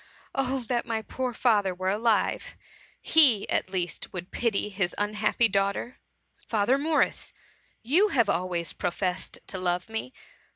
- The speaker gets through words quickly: No, average, 140 wpm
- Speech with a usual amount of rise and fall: Yes, average, 4.7 semitones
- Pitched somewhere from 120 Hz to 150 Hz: No, high, 210 Hz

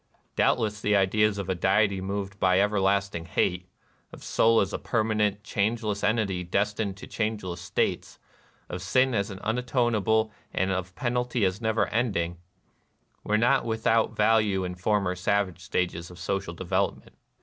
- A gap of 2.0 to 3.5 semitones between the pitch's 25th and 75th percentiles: Yes, average, 2.9 semitones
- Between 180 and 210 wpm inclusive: No, average, 160 wpm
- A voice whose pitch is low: Yes, low, 100 Hz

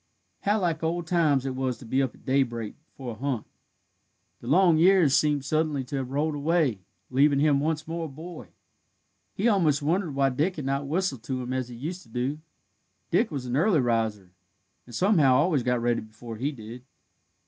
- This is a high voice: No, medium, 140 Hz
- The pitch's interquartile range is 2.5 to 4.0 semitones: No, average, 4.4 semitones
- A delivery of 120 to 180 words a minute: No, average, 195 wpm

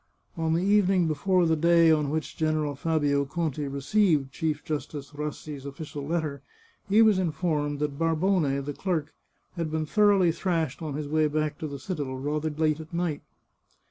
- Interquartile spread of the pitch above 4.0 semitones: No, narrow, 2.5 semitones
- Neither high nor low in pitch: Yes, medium, 155 Hz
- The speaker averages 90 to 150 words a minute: No, average, 170 wpm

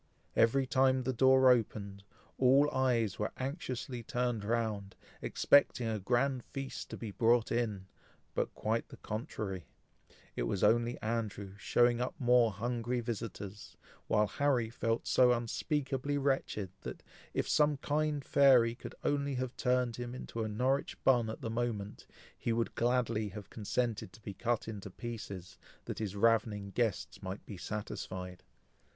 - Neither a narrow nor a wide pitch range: Yes, average, 3.2 semitones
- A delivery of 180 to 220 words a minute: No, average, 150 wpm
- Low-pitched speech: Yes, low, 115 Hz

